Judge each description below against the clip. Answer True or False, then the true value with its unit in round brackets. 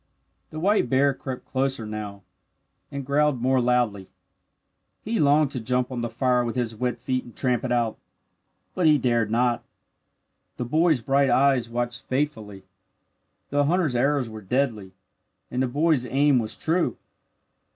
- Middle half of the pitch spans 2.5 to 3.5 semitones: True (3.1 semitones)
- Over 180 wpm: False (155 wpm)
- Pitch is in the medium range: False (125 Hz)